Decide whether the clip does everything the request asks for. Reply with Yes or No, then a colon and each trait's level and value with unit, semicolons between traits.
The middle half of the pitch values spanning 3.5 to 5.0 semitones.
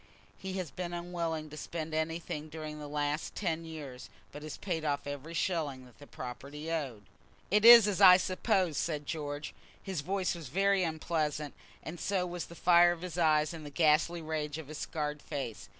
No: average, 2.8 semitones